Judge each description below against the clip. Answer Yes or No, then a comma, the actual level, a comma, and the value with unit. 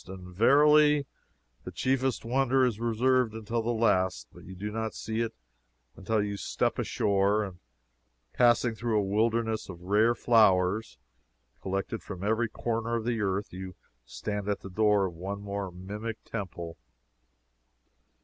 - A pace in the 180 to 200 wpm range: No, average, 150 wpm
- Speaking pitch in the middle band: No, low, 110 Hz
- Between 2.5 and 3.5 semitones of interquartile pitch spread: Yes, average, 3.1 semitones